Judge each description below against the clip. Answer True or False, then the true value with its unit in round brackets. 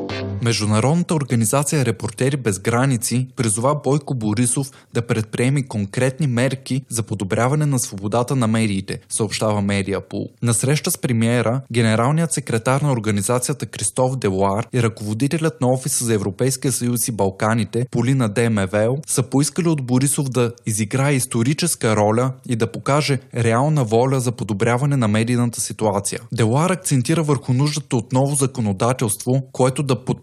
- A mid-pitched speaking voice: False (125 Hz)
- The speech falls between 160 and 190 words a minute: False (135 wpm)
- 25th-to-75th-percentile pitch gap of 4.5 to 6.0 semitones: False (3.3 semitones)